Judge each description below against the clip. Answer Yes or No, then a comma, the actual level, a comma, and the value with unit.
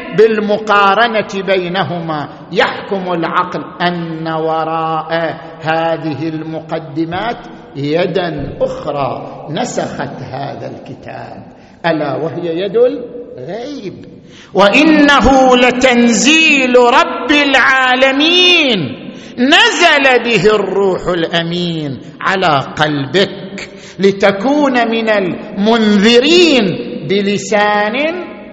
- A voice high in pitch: Yes, high, 200 Hz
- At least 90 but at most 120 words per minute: No, slow, 65 wpm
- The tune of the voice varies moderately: No, wide, 7.0 semitones